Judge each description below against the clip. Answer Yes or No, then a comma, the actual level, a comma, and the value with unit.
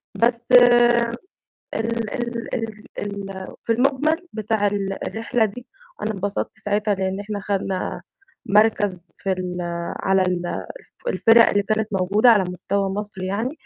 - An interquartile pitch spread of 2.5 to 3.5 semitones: Yes, average, 3.2 semitones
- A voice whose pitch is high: Yes, high, 210 Hz